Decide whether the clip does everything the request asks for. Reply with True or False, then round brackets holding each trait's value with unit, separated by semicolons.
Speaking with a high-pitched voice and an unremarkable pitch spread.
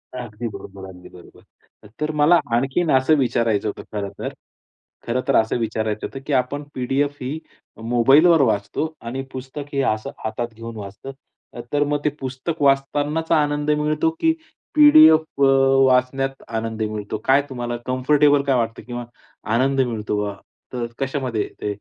False (130 Hz; 4.3 semitones)